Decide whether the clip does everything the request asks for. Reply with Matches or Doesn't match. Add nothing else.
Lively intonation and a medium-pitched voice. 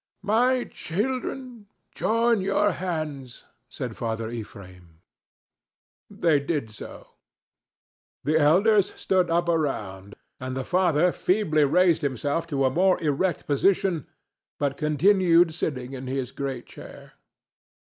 Matches